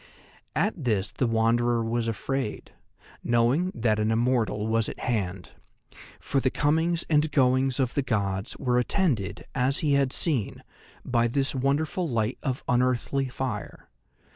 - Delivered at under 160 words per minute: Yes, average, 140 wpm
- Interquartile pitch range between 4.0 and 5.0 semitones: No, average, 3.3 semitones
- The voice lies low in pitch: Yes, low, 125 Hz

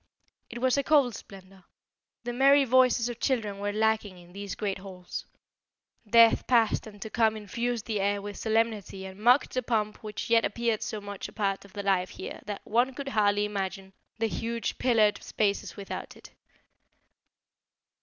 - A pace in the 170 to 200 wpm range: Yes, average, 175 wpm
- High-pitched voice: Yes, high, 215 Hz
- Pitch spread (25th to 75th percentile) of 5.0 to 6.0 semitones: No, average, 2.9 semitones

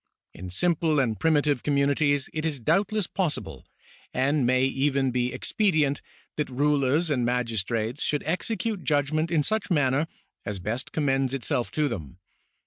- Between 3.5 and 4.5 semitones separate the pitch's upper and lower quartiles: Yes, average, 3.8 semitones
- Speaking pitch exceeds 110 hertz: Yes, medium, 140 Hz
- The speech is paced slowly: No, average, 150 wpm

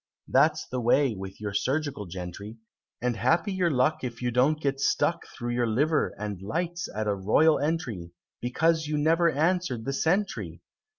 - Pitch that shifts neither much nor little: No, wide, 6.7 semitones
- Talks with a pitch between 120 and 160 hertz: Yes, low, 135 Hz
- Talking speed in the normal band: Yes, average, 170 wpm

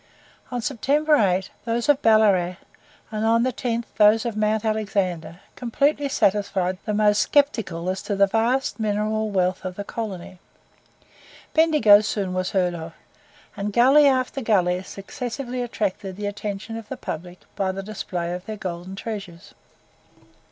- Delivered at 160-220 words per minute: No, average, 150 wpm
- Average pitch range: Yes, average, 3.7 semitones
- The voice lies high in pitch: Yes, high, 210 Hz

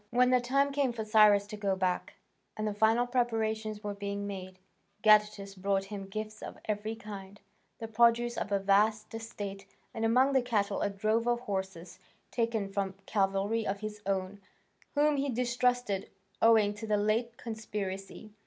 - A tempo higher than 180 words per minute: No, average, 165 wpm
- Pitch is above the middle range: Yes, high, 215 Hz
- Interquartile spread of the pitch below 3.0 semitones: Yes, narrow, 2.5 semitones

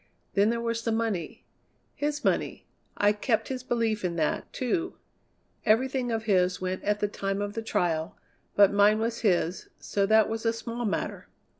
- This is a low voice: No, high, 215 Hz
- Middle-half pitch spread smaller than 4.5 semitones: Yes, average, 2.7 semitones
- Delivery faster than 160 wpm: Yes, average, 175 wpm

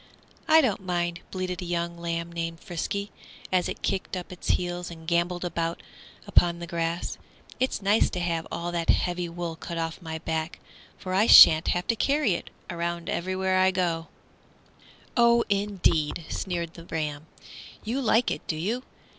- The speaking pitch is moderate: Yes, medium, 175 Hz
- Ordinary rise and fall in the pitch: No, narrow, 2.0 semitones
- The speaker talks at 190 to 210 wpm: No, average, 170 wpm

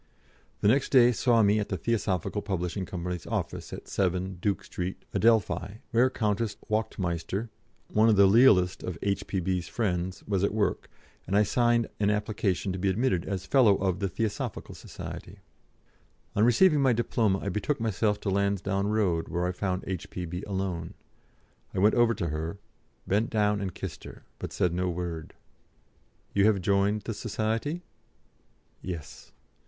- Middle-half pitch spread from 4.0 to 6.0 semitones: No, average, 3.2 semitones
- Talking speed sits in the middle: Yes, average, 160 wpm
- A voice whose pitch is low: Yes, low, 100 Hz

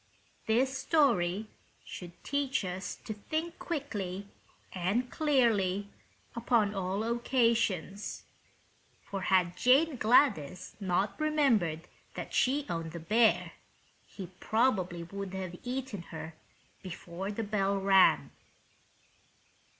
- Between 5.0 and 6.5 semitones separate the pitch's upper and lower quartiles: Yes, wide, 5.4 semitones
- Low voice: No, high, 205 Hz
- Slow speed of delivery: Yes, slow, 105 wpm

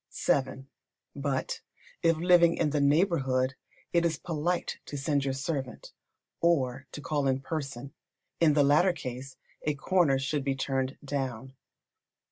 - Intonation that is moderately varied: Yes, average, 3.2 semitones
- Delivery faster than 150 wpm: No, average, 140 wpm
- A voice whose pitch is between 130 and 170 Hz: Yes, medium, 140 Hz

